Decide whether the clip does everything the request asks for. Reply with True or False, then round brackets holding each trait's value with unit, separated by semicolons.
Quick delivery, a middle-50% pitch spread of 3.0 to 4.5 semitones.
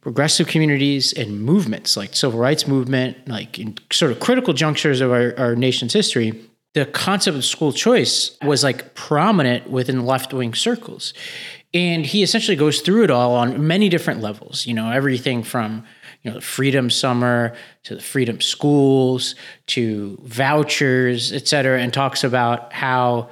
False (160 wpm; 3.9 semitones)